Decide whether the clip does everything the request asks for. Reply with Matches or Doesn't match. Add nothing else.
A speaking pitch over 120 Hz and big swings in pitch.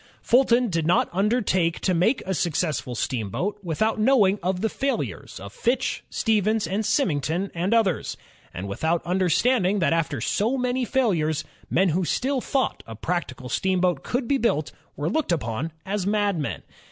Matches